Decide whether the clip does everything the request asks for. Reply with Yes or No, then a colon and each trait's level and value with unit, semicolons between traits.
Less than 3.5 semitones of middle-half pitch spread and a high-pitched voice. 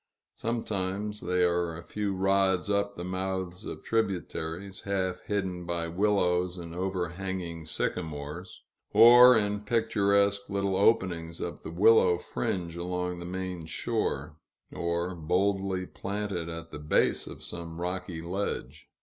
No: narrow, 2.5 semitones; very low, 90 Hz